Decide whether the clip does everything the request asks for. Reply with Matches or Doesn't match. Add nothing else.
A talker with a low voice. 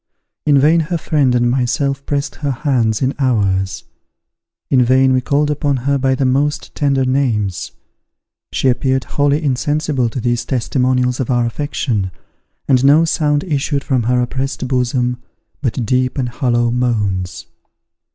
Matches